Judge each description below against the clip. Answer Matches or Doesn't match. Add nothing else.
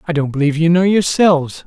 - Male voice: Matches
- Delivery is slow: Doesn't match